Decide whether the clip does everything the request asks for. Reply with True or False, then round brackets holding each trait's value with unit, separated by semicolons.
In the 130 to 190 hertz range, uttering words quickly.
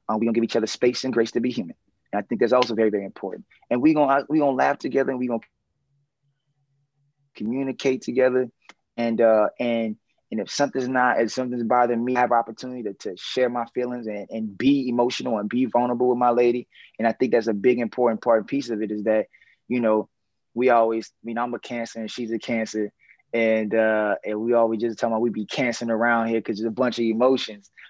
False (120 Hz; 230 wpm)